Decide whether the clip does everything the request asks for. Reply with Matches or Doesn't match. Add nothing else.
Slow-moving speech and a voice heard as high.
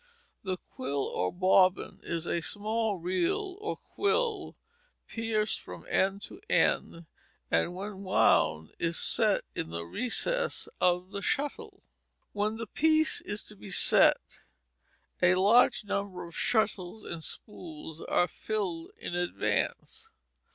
Matches